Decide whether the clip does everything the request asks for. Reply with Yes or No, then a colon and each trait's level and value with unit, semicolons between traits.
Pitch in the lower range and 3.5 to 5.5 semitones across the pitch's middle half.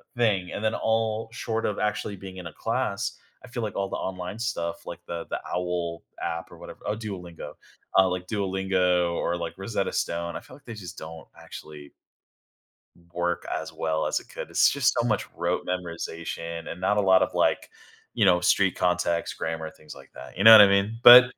Yes: very low, 95 Hz; average, 3.9 semitones